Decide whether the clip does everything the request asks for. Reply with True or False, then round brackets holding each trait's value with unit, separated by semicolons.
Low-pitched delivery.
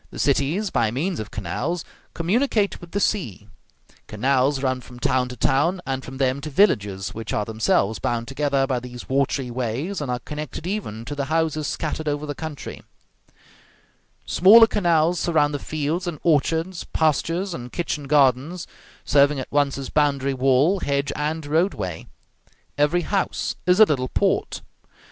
False (145 Hz)